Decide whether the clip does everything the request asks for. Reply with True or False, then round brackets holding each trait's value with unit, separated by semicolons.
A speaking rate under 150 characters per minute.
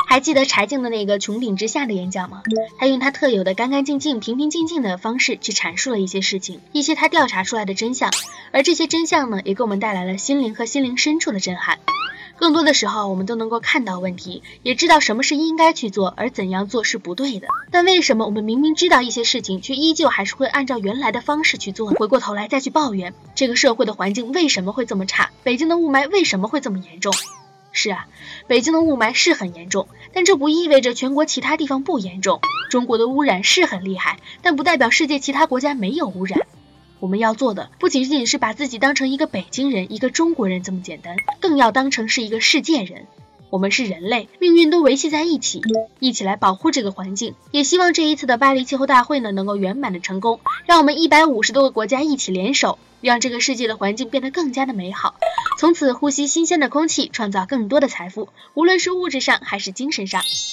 False (355 characters per minute)